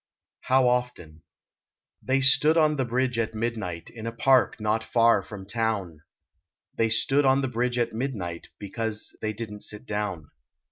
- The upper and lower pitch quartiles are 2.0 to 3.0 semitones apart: No, average, 3.4 semitones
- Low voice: Yes, low, 115 Hz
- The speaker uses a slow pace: No, average, 160 wpm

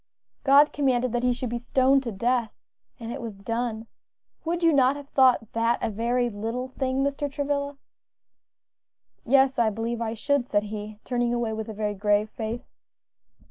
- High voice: Yes, high, 240 Hz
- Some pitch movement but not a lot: Yes, average, 3.3 semitones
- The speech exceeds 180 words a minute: No, average, 175 wpm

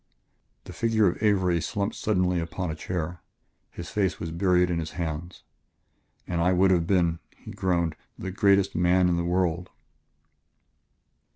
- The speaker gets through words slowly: No, average, 155 wpm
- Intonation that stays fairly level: Yes, narrow, 1.7 semitones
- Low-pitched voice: Yes, very low, 90 Hz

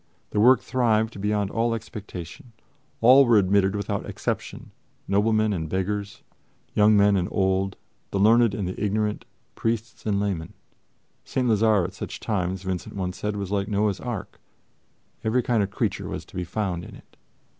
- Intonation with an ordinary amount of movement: No, narrow, 2.3 semitones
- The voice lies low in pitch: Yes, low, 105 Hz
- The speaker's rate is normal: Yes, average, 165 wpm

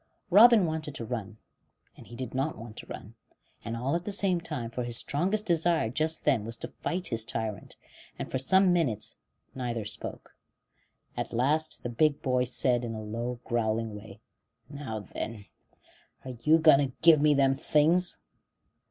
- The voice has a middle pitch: No, low, 130 Hz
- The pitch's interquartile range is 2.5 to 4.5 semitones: No, wide, 5.5 semitones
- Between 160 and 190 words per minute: Yes, average, 175 wpm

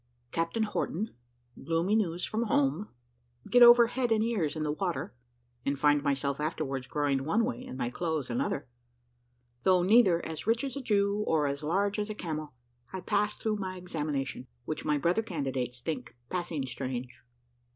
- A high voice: No, medium, 165 Hz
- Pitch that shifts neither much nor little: No, wide, 6.6 semitones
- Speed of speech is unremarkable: Yes, average, 170 wpm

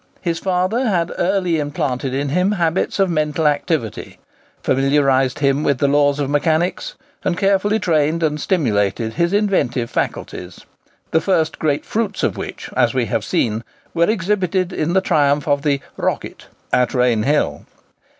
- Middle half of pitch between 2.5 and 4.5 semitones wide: No, average, 4.9 semitones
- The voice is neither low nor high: Yes, medium, 155 Hz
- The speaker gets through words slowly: No, average, 150 wpm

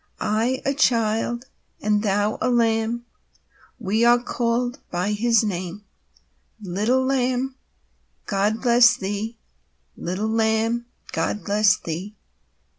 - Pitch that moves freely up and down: No, narrow, 2.6 semitones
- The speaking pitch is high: Yes, high, 225 Hz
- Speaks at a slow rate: Yes, slow, 110 wpm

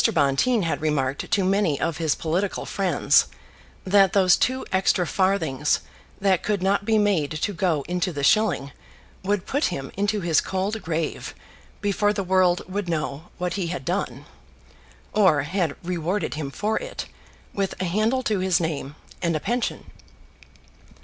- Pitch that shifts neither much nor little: Yes, average, 4.1 semitones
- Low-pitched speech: No, medium, 185 Hz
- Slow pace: No, average, 155 wpm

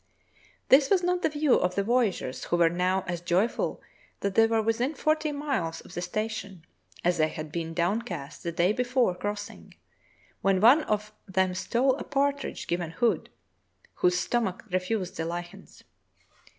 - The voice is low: No, high, 200 Hz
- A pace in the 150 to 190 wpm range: Yes, average, 165 wpm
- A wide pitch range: Yes, wide, 5.8 semitones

